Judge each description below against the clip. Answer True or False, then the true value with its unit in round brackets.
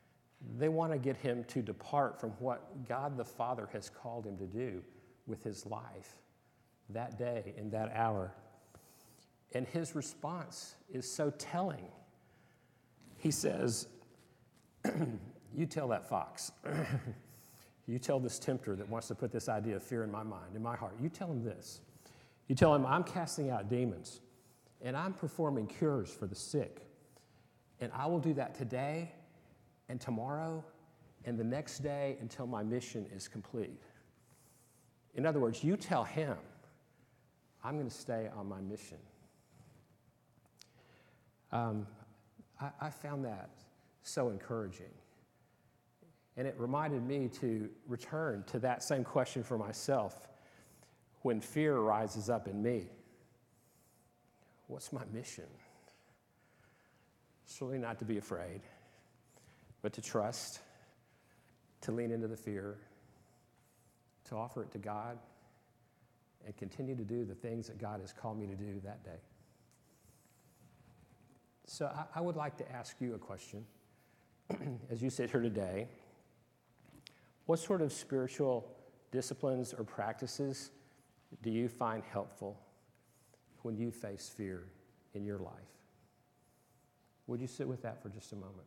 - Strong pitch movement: False (3.7 semitones)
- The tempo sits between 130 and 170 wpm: True (140 wpm)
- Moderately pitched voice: False (120 Hz)